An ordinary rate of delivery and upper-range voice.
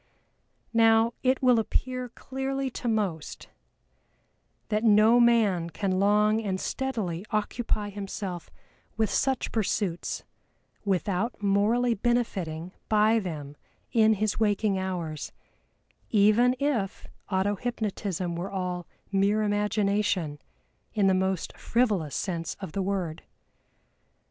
No: slow, 110 wpm; high, 205 Hz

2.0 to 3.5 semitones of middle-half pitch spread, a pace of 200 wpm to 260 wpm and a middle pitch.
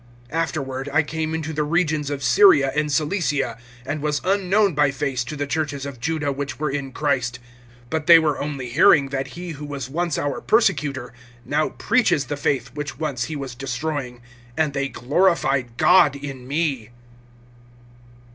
No: average, 2.7 semitones; average, 165 wpm; medium, 145 Hz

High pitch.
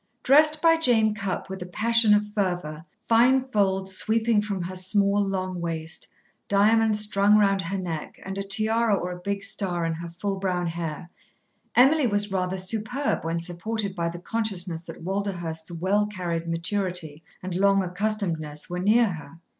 Yes: high, 195 Hz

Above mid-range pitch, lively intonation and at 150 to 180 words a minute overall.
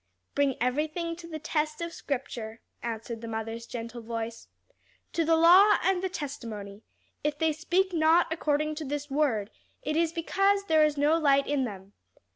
Yes: very high, 295 Hz; wide, 5.9 semitones; average, 170 wpm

